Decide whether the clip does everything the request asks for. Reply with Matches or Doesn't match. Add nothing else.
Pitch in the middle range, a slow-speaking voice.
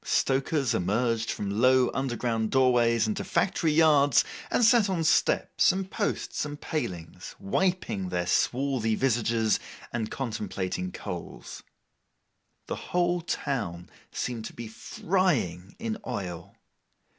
Doesn't match